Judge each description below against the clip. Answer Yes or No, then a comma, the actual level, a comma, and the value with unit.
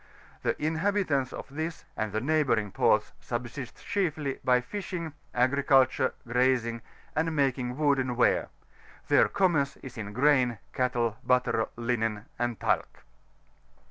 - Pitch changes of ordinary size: Yes, average, 4.0 semitones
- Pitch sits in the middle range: No, low, 130 Hz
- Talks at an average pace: No, slow, 120 wpm